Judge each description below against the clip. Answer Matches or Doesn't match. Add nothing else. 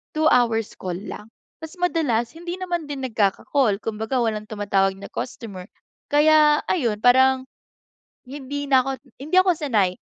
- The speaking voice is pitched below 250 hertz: Doesn't match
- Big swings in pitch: Matches